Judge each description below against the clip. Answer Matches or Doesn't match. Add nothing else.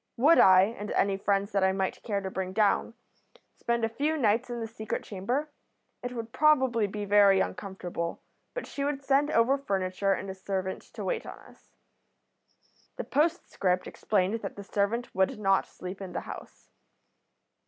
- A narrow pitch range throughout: Doesn't match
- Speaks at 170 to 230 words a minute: Matches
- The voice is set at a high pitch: Matches